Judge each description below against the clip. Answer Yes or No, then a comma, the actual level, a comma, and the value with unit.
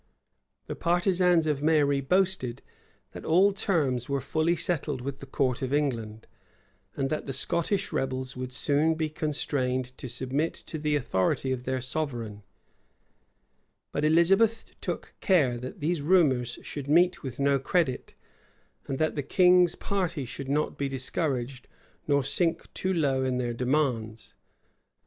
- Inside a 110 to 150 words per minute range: Yes, average, 145 wpm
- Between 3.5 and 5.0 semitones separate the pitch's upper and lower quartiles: Yes, average, 4.3 semitones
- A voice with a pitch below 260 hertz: Yes, medium, 140 Hz